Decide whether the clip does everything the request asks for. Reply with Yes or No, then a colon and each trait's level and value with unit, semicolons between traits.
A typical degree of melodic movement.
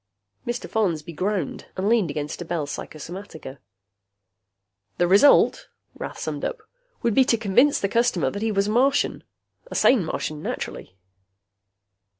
No: wide, 6.5 semitones